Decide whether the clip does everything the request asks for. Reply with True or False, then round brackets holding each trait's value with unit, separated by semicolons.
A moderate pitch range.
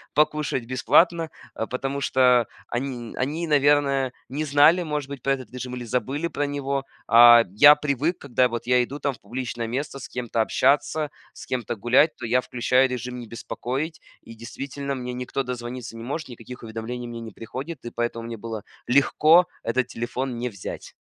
True (3.1 semitones)